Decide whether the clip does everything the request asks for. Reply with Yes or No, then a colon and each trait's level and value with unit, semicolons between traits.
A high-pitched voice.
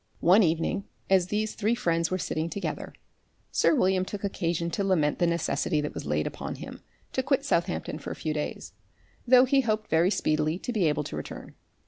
No: medium, 180 Hz